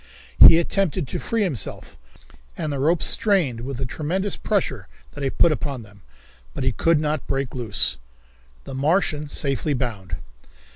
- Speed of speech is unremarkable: Yes, average, 155 wpm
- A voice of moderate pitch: Yes, medium, 145 Hz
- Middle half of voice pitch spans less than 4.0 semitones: No, average, 4.6 semitones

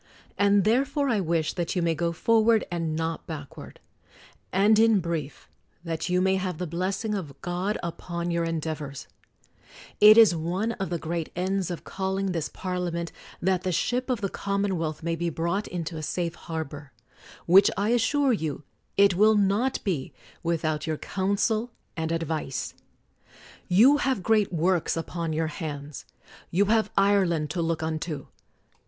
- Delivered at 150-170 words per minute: Yes, average, 160 wpm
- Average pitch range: Yes, average, 3.7 semitones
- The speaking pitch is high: No, medium, 175 Hz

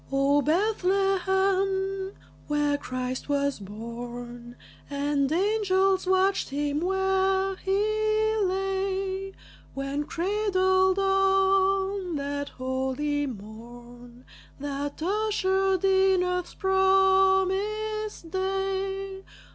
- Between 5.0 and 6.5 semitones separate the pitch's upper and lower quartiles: Yes, average, 5.3 semitones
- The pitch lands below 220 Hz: No, very high, 380 Hz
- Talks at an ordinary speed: No, slow, 75 wpm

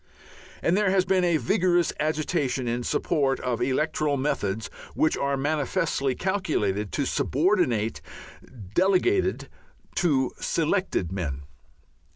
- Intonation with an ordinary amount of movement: No, wide, 6.0 semitones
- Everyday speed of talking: No, slow, 110 wpm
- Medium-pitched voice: Yes, medium, 150 Hz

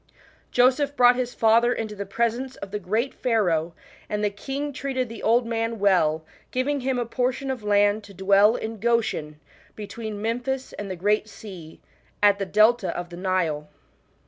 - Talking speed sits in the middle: Yes, average, 170 wpm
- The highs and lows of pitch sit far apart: No, average, 3.7 semitones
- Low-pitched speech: No, high, 220 Hz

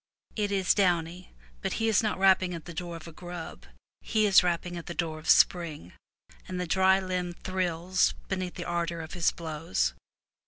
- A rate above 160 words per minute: Yes, average, 190 wpm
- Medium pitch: Yes, medium, 175 Hz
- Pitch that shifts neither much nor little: No, narrow, 2.0 semitones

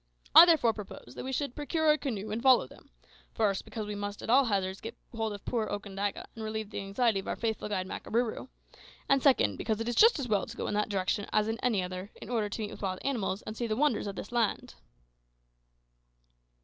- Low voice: No, high, 220 Hz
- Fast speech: Yes, fast, 230 wpm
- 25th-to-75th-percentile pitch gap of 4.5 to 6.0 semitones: No, average, 3.1 semitones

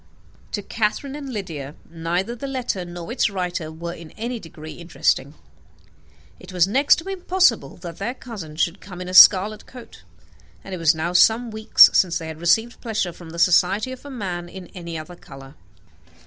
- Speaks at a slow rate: No, average, 185 wpm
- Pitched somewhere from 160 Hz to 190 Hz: Yes, medium, 185 Hz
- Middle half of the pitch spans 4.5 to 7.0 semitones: Yes, average, 5.2 semitones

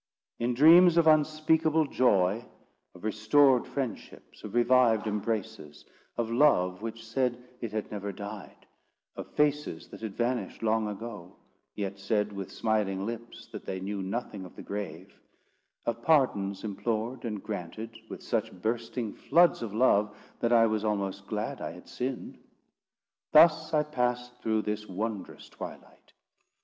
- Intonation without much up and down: No, average, 3.5 semitones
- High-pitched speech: No, low, 110 Hz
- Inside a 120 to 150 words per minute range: Yes, average, 140 wpm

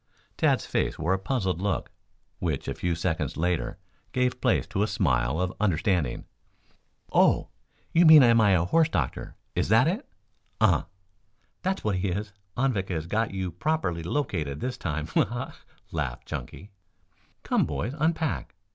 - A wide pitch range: Yes, wide, 6.5 semitones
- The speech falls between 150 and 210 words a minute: Yes, average, 155 wpm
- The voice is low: Yes, very low, 95 Hz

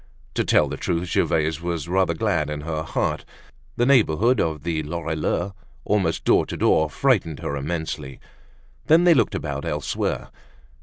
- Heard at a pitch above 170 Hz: No, very low, 85 Hz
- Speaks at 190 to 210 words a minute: No, average, 155 wpm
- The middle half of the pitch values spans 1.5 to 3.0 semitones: No, average, 4.4 semitones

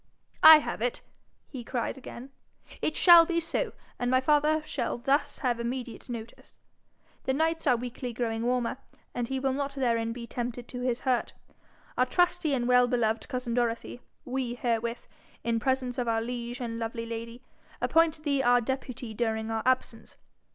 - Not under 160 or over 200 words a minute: Yes, average, 170 wpm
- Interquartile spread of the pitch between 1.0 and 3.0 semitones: Yes, narrow, 2.4 semitones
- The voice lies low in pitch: No, high, 245 Hz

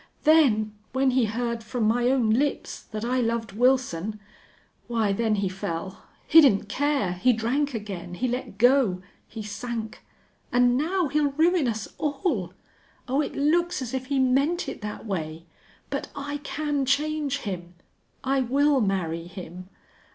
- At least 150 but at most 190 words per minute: Yes, average, 155 wpm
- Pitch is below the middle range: No, high, 245 Hz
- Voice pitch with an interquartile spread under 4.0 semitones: No, average, 5.1 semitones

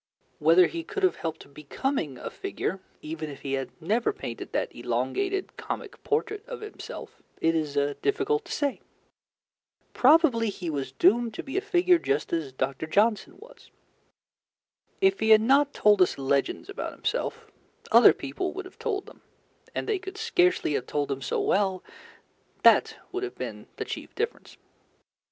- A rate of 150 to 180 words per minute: Yes, average, 165 wpm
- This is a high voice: Yes, high, 235 Hz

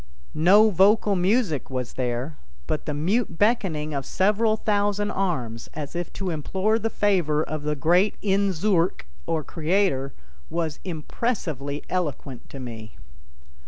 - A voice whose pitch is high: No, medium, 170 Hz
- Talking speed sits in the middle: No, slow, 130 wpm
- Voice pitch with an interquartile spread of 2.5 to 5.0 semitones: No, wide, 5.5 semitones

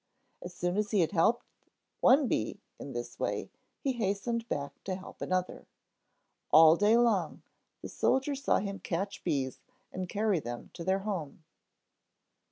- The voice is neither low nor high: No, high, 195 Hz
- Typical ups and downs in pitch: Yes, average, 4.4 semitones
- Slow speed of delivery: No, average, 155 wpm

